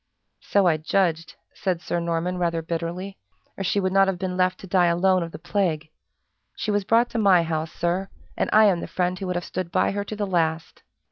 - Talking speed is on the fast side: Yes, fast, 225 wpm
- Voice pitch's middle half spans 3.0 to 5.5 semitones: No, narrow, 2.5 semitones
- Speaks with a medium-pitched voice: Yes, medium, 180 Hz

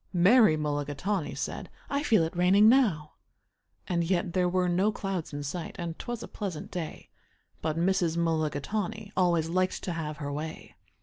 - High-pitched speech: No, medium, 175 Hz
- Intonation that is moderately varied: Yes, average, 3.6 semitones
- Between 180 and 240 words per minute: No, average, 165 wpm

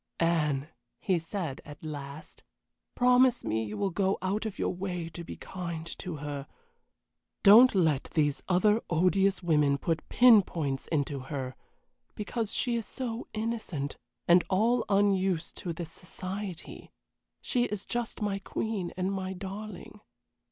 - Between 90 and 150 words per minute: Yes, average, 145 wpm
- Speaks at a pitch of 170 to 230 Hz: Yes, medium, 185 Hz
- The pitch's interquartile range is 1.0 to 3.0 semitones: No, average, 4.9 semitones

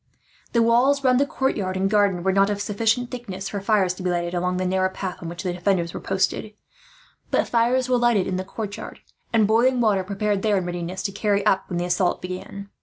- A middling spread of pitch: Yes, average, 3.5 semitones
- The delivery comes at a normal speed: No, fast, 225 wpm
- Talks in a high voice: Yes, high, 200 Hz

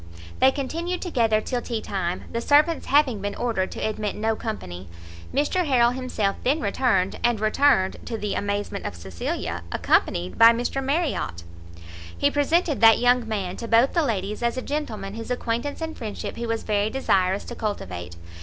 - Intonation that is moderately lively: Yes, average, 4.7 semitones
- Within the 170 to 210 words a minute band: Yes, average, 175 wpm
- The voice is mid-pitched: No, high, 230 Hz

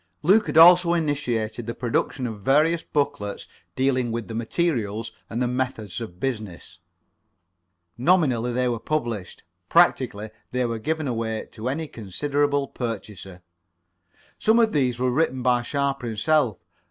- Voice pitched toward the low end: Yes, low, 125 Hz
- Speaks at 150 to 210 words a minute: No, average, 140 wpm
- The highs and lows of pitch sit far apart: No, average, 4.4 semitones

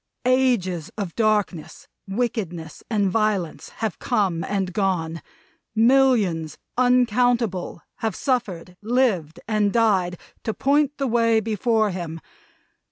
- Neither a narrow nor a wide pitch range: Yes, average, 5.0 semitones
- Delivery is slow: Yes, slow, 105 wpm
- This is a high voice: Yes, high, 215 Hz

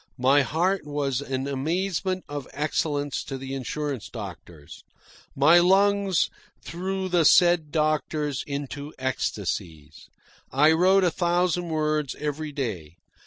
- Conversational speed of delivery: No, slow, 120 wpm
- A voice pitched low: No, medium, 150 Hz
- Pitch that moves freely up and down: No, average, 4.3 semitones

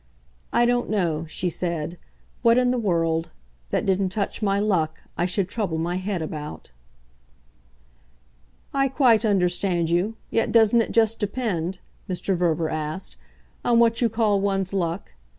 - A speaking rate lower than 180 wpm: Yes, average, 150 wpm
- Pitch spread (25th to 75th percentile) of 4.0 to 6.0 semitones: Yes, average, 4.8 semitones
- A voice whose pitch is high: Yes, high, 195 Hz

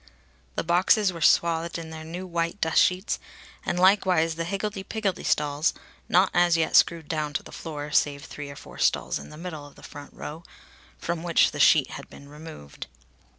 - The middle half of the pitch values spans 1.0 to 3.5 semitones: Yes, average, 2.8 semitones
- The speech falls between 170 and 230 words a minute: Yes, average, 195 wpm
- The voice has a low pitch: No, medium, 165 Hz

